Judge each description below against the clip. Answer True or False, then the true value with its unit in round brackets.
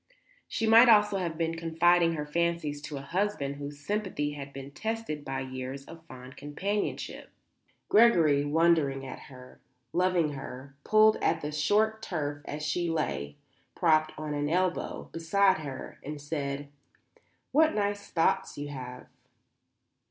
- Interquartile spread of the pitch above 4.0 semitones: True (4.4 semitones)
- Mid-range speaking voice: True (155 Hz)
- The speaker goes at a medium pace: True (145 wpm)